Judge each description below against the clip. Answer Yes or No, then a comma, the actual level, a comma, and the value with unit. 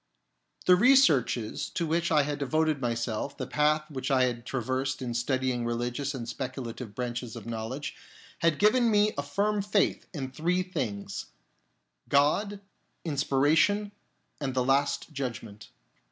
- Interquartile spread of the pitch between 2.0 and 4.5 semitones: No, average, 4.9 semitones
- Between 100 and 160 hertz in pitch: Yes, medium, 140 Hz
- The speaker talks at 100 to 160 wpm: Yes, average, 140 wpm